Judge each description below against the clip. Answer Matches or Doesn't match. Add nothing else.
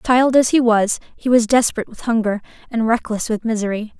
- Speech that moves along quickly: Doesn't match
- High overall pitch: Matches